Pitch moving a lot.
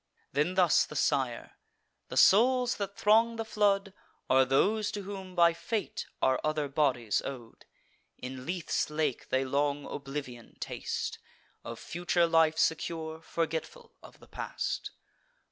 Yes: wide, 6.1 semitones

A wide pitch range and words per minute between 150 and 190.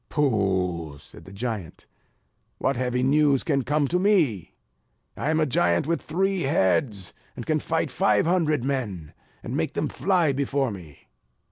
Yes: wide, 7.8 semitones; average, 155 wpm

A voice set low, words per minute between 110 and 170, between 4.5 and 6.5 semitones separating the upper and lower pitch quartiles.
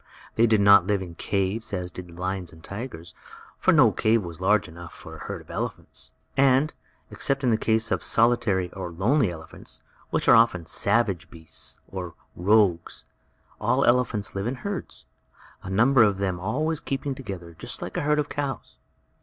No: low, 100 Hz; average, 180 wpm; average, 5.0 semitones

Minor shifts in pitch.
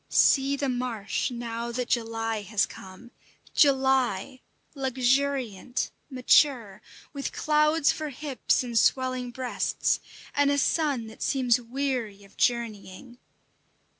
No: average, 3.2 semitones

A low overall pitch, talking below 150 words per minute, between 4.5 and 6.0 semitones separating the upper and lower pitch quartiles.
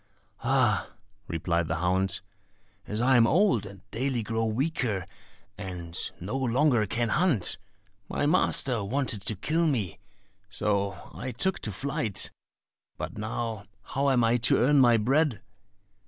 Yes: low, 115 Hz; average, 140 wpm; average, 5.1 semitones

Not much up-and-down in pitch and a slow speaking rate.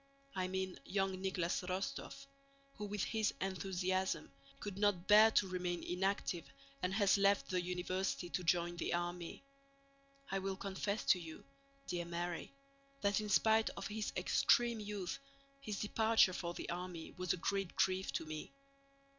No: narrow, 2.3 semitones; average, 155 wpm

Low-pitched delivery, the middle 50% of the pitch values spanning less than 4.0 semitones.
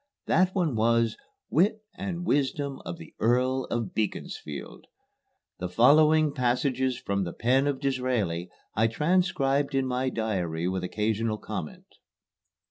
No: low, 125 Hz; average, 4.8 semitones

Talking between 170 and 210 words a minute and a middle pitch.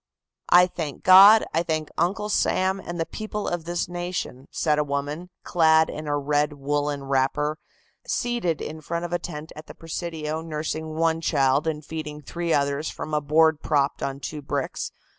Yes: average, 180 wpm; medium, 155 Hz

